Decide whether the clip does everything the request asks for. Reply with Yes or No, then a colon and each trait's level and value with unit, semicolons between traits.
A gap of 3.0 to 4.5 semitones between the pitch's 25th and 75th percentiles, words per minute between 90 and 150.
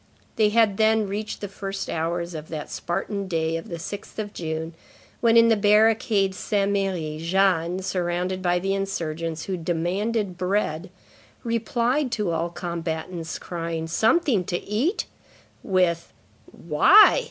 Yes: average, 3.9 semitones; average, 140 wpm